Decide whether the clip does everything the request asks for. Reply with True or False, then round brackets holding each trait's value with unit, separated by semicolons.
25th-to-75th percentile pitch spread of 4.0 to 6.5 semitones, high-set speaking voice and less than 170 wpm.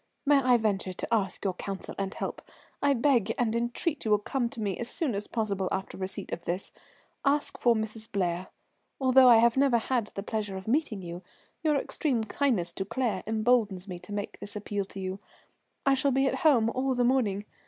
False (4.7 semitones; 220 Hz; 205 wpm)